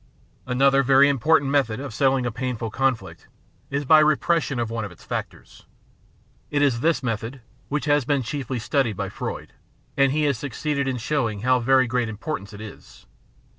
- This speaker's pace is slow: No, average, 185 wpm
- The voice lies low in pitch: Yes, low, 130 Hz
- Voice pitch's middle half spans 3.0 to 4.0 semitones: Yes, average, 3.5 semitones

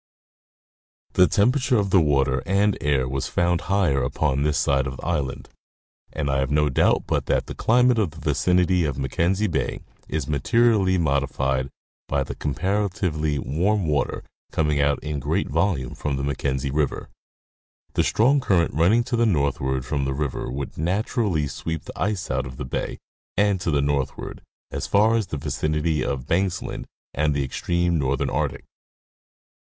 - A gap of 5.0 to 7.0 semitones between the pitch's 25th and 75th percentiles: Yes, wide, 5.6 semitones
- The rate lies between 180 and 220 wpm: No, average, 170 wpm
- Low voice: Yes, very low, 75 Hz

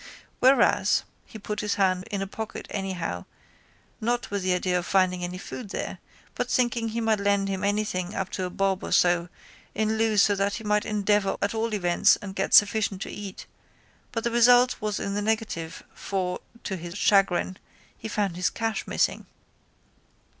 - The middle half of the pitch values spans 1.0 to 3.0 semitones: Yes, average, 2.7 semitones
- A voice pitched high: Yes, high, 200 Hz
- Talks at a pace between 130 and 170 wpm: No, average, 180 wpm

